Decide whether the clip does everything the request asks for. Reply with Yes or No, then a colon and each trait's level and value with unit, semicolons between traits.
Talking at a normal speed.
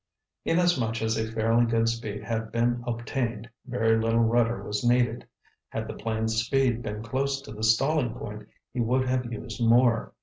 Yes: average, 170 wpm